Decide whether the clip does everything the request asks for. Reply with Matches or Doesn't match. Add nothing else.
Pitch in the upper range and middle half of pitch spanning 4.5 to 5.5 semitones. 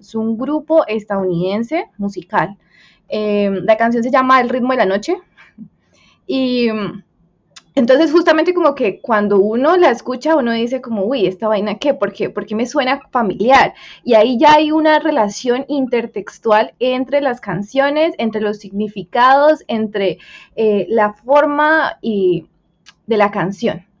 Matches